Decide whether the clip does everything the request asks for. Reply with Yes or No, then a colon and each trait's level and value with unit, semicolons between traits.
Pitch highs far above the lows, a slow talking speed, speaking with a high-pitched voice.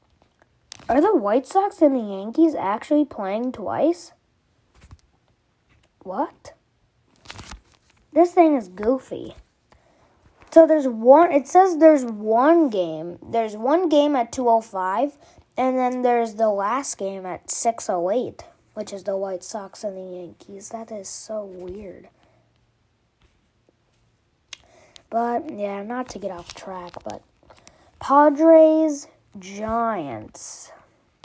Yes: wide, 7.0 semitones; slow, 110 wpm; high, 225 Hz